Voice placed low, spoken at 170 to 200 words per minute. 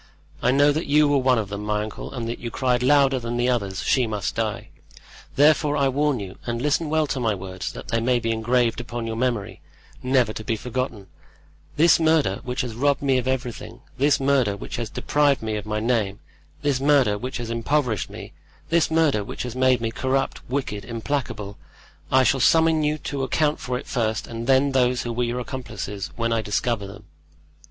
Yes: low, 125 Hz; average, 195 wpm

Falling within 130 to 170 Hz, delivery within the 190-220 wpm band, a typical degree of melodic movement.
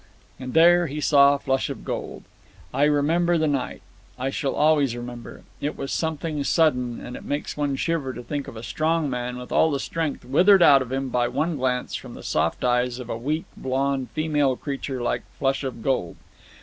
Yes: medium, 140 Hz; average, 200 wpm; average, 3.4 semitones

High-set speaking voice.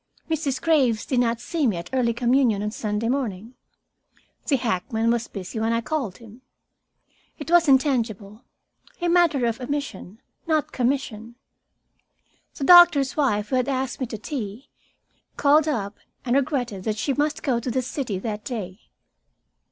Yes: high, 245 Hz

